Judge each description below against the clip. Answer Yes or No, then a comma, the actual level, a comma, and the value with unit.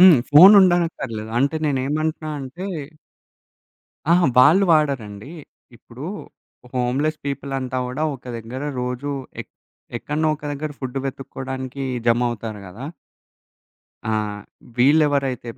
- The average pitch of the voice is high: No, low, 135 Hz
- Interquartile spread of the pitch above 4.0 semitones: No, average, 3.7 semitones